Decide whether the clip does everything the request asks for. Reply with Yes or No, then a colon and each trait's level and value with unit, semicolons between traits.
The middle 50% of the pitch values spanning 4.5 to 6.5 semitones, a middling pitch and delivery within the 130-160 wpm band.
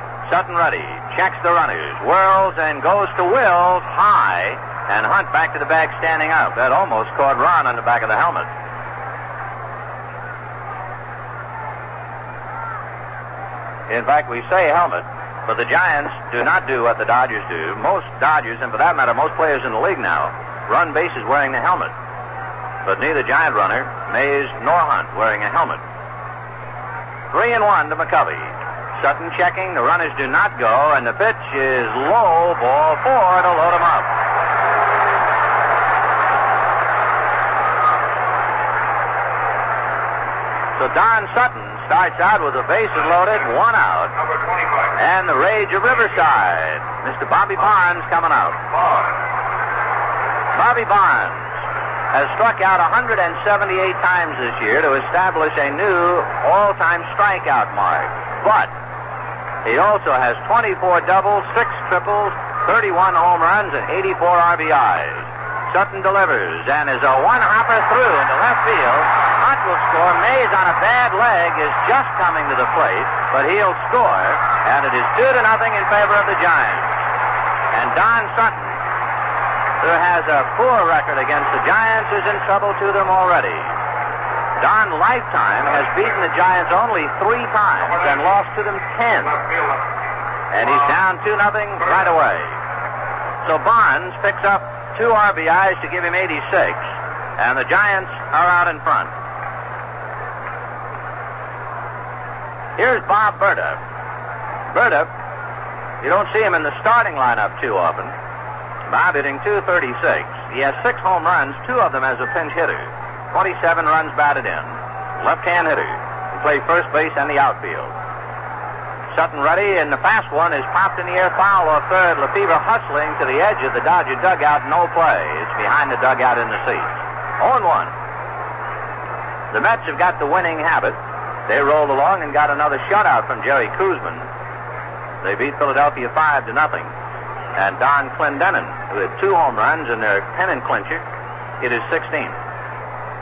Yes: wide, 5.4 semitones; medium, 175 Hz; average, 150 wpm